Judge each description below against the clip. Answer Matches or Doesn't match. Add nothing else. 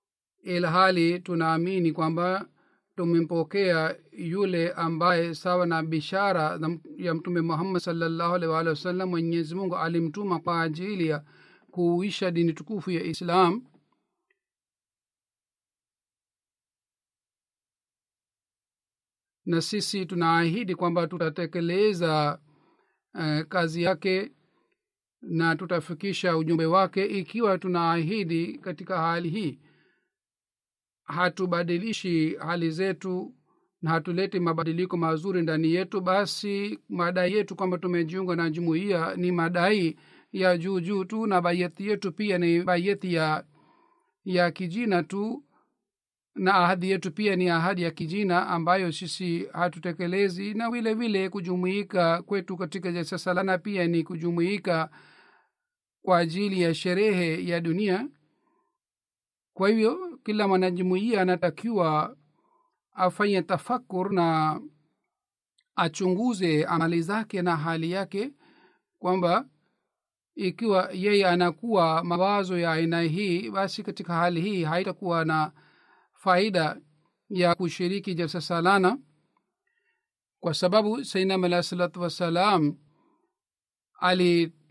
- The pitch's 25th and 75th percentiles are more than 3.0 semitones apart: Doesn't match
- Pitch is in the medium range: Matches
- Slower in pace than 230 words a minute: Matches